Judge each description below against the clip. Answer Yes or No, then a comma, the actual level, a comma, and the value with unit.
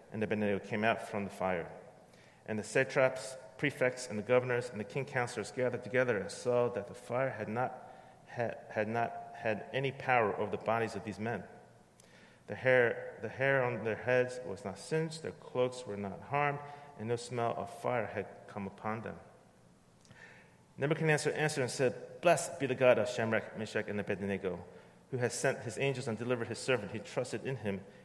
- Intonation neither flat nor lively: Yes, average, 3.8 semitones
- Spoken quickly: No, average, 190 wpm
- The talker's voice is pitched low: Yes, low, 120 Hz